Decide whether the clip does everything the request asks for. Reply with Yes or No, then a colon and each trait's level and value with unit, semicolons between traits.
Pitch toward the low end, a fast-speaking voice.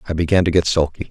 Yes: very low, 85 Hz; fast, 270 wpm